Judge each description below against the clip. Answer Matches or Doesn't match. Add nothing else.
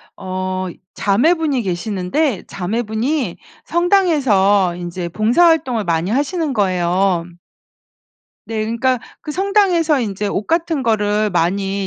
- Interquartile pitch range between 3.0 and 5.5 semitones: Doesn't match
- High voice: Matches